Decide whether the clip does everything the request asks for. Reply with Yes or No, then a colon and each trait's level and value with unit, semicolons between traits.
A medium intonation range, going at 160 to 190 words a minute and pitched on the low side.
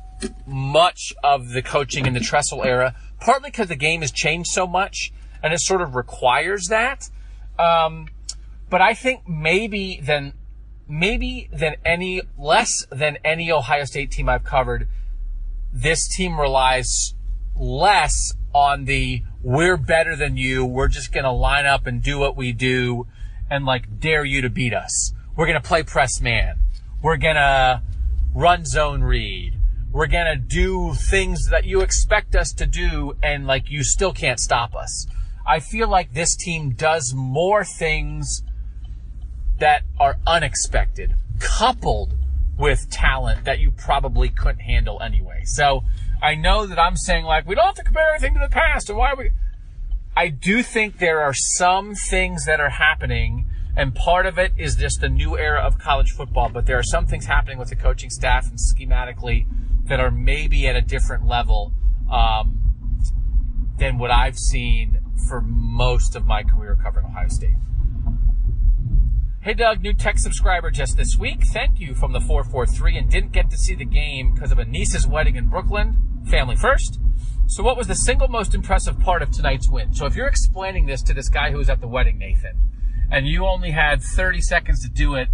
No: wide, 6.6 semitones; average, 175 wpm; low, 130 Hz